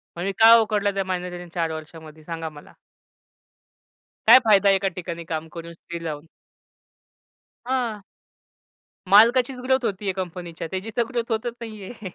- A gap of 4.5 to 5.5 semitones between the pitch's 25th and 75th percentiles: Yes, average, 4.9 semitones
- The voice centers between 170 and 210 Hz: Yes, high, 190 Hz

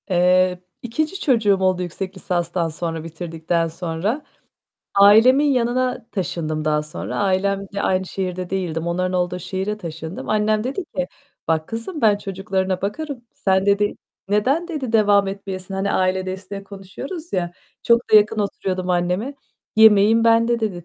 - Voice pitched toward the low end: No, high, 195 Hz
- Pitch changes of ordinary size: Yes, average, 3.4 semitones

